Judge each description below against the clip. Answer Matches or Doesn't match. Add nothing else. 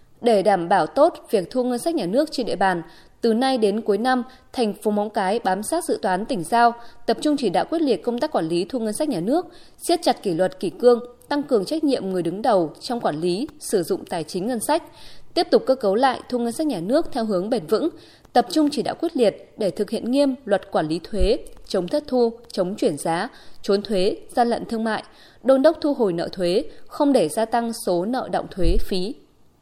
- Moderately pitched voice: Doesn't match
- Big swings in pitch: Matches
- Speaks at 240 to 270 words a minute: Matches